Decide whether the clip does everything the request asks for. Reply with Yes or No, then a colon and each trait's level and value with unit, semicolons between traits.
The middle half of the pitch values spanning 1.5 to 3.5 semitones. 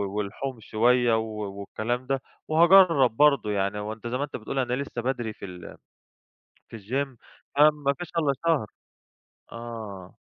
No: average, 4.5 semitones